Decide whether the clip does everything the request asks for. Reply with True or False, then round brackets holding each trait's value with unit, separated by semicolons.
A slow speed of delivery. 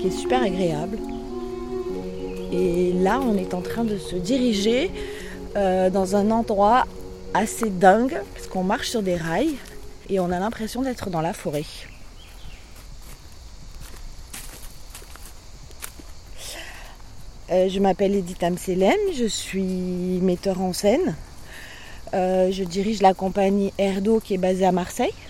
True (130 wpm)